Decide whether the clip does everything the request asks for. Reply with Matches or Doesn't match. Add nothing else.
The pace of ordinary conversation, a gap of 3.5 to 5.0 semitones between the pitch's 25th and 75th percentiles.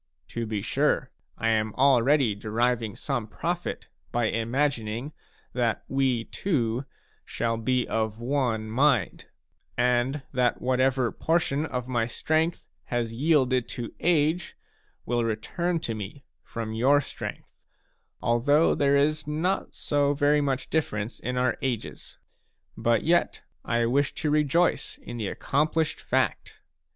Doesn't match